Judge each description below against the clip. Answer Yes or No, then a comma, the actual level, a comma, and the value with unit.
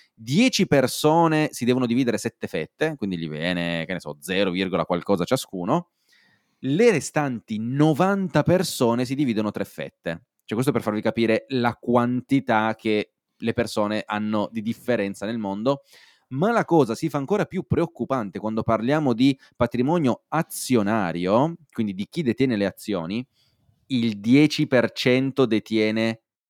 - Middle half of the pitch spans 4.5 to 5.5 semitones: Yes, average, 5.1 semitones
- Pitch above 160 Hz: No, low, 120 Hz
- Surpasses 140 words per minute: No, average, 135 wpm